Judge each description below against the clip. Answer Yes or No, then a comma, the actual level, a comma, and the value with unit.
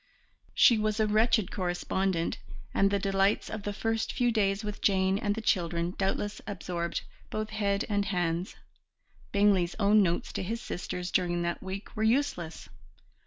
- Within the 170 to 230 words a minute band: No, average, 160 wpm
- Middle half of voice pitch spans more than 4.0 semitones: No, average, 3.0 semitones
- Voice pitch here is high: Yes, high, 200 Hz